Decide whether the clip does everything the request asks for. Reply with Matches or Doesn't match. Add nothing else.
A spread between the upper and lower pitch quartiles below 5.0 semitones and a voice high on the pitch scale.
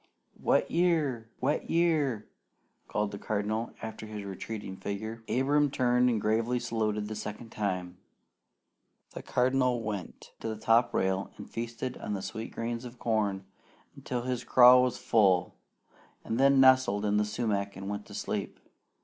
Doesn't match